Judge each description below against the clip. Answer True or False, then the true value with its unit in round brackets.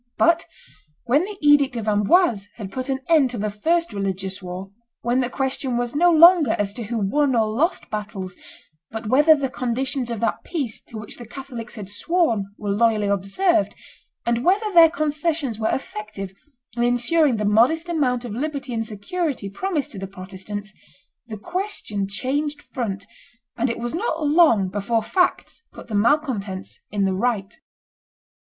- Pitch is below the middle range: False (240 Hz)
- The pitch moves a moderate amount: False (6.4 semitones)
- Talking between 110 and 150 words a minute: False (170 wpm)